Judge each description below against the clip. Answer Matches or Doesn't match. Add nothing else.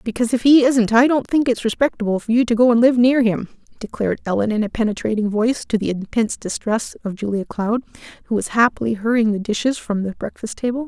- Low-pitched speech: Doesn't match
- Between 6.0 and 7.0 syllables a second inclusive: Matches